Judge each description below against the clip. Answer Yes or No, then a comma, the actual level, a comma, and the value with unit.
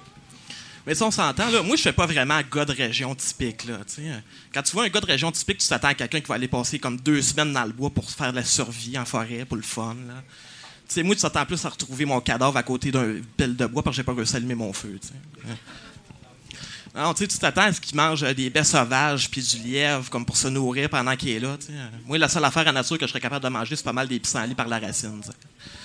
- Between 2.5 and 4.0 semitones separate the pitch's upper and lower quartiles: Yes, average, 3.6 semitones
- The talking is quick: Yes, fast, 275 wpm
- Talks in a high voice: No, low, 135 Hz